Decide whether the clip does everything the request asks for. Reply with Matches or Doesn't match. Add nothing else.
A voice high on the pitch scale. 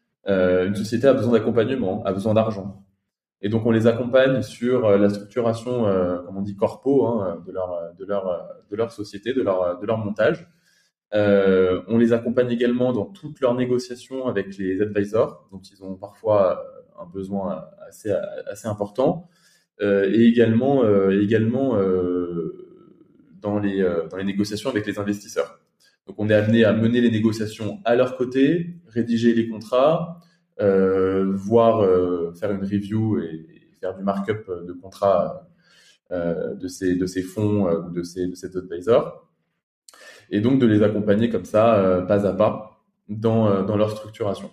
Doesn't match